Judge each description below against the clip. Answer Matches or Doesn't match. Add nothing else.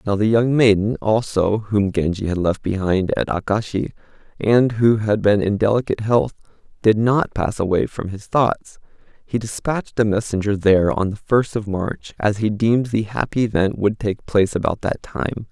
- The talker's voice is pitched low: Matches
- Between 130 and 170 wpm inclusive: Doesn't match